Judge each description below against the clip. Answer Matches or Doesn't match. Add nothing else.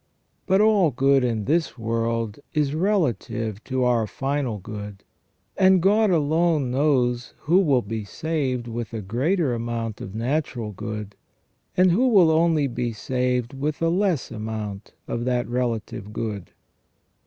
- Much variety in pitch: Matches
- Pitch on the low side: Matches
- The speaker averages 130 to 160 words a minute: Matches